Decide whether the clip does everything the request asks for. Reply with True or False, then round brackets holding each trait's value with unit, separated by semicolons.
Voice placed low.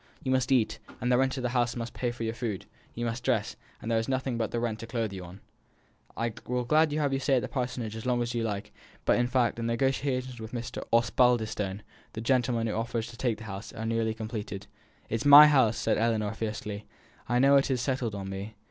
True (115 Hz)